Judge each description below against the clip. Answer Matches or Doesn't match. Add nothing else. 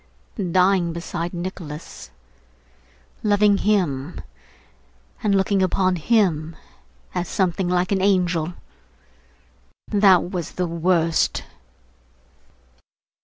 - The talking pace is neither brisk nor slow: Doesn't match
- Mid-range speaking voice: Matches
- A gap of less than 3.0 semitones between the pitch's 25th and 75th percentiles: Matches